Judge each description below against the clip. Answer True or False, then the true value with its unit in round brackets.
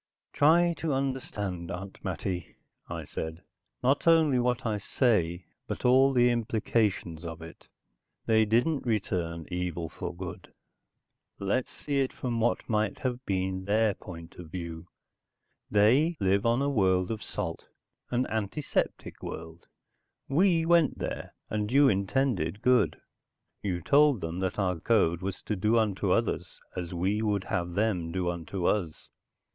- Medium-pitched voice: False (105 Hz)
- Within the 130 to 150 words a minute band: True (145 wpm)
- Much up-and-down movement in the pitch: True (5.7 semitones)